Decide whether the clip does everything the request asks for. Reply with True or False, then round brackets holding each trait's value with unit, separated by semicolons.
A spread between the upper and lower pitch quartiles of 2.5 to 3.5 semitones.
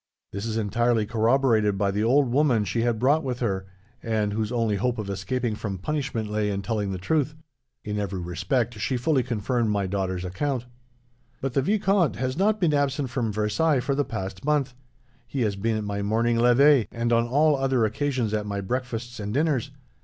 False (4.4 semitones)